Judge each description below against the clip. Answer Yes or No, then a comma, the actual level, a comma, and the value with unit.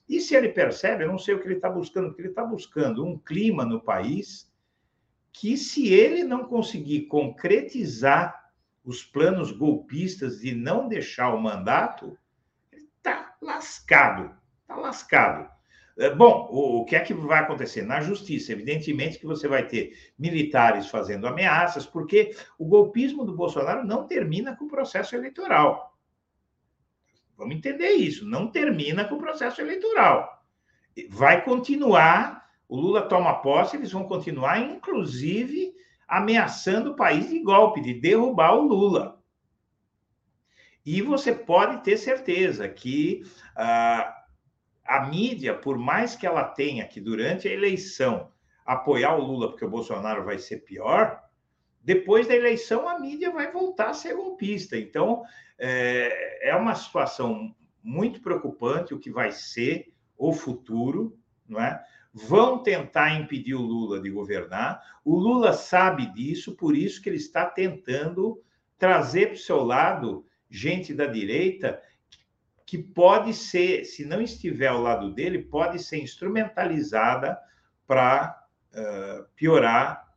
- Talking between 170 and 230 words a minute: No, average, 140 wpm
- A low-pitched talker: No, high, 195 Hz